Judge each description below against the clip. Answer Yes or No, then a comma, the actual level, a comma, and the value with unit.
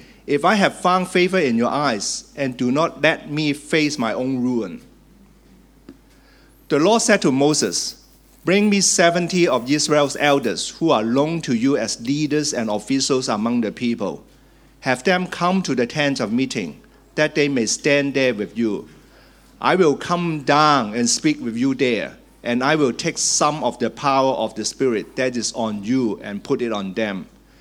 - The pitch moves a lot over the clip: Yes, wide, 6.0 semitones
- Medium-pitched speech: Yes, medium, 145 Hz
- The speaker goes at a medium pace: Yes, average, 185 wpm